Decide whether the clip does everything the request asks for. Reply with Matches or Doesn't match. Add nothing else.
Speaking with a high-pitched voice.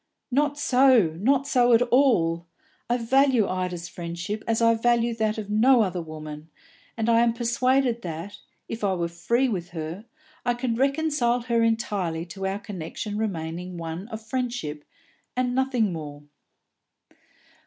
Matches